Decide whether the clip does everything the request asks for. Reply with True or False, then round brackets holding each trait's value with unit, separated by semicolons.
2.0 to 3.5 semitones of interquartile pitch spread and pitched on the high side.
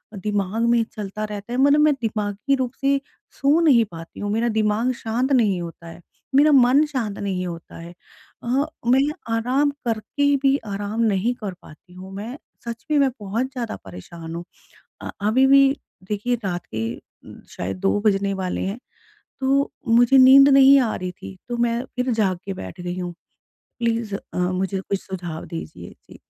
False (5.3 semitones; 220 Hz)